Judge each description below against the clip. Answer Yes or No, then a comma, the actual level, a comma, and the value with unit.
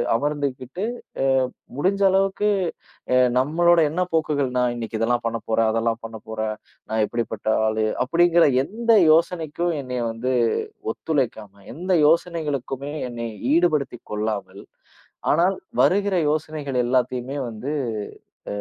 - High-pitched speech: No, low, 135 Hz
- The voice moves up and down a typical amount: No, wide, 6.4 semitones